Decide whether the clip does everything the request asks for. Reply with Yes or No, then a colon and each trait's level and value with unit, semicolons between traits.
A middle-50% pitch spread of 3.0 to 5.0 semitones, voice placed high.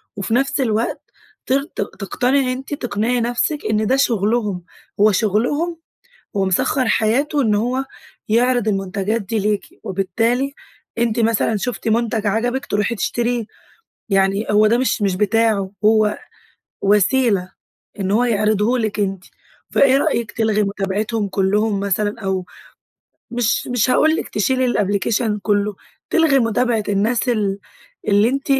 Yes: average, 3.3 semitones; high, 220 Hz